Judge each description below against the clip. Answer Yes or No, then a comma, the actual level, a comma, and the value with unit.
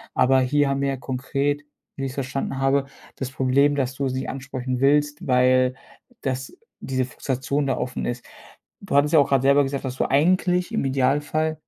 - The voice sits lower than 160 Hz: Yes, low, 135 Hz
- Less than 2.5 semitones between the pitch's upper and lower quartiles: Yes, narrow, 1.7 semitones